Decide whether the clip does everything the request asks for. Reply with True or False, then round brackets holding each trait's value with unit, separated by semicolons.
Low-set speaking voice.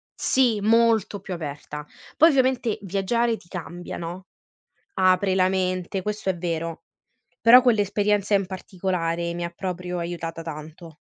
False (185 Hz)